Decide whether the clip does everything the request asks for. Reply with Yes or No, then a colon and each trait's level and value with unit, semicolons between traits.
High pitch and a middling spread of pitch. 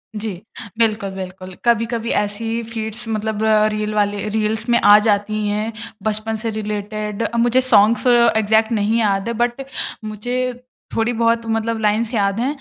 No: high, 220 Hz; narrow, 1.7 semitones